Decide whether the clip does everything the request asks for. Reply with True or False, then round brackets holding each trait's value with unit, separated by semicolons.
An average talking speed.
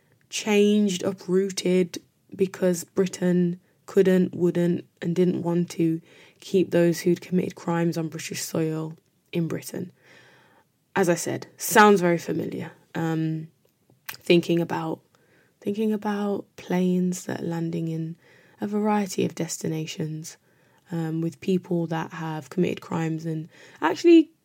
False (120 wpm)